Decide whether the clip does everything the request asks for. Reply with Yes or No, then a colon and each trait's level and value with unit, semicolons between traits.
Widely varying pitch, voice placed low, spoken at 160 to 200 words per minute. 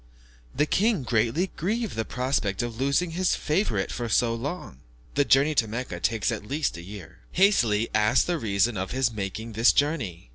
Yes: wide, 6.1 semitones; low, 120 Hz; average, 185 wpm